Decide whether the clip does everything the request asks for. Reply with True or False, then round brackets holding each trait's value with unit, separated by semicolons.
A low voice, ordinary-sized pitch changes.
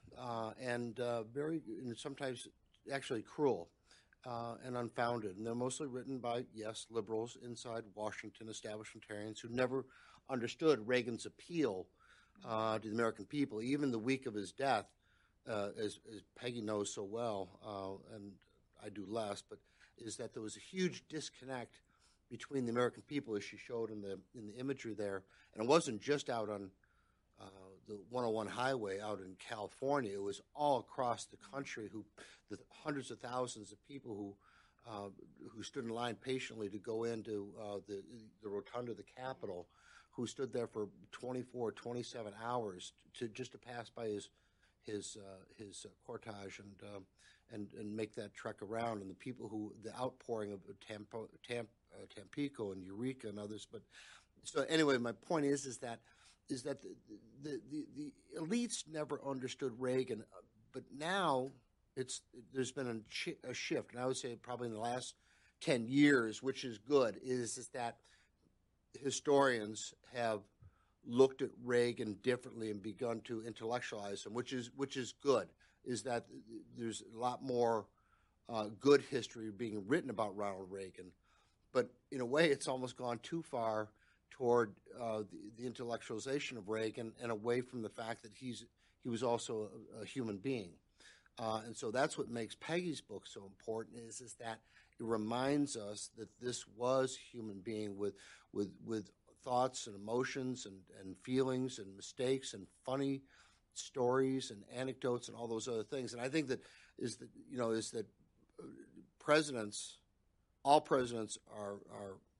True (115 Hz; 3.4 semitones)